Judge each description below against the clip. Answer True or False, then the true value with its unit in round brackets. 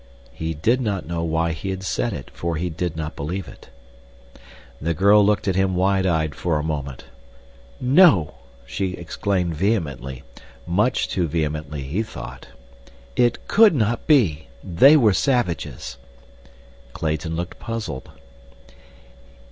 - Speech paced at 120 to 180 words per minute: True (135 wpm)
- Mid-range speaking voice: False (85 Hz)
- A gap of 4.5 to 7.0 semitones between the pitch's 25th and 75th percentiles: True (4.8 semitones)